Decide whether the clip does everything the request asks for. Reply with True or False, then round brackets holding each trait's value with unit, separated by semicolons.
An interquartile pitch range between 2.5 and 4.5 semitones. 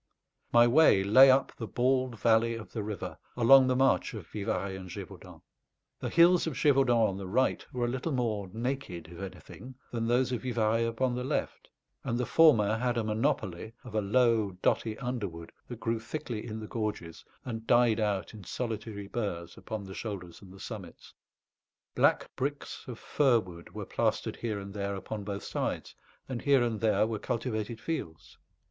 True (3.5 semitones)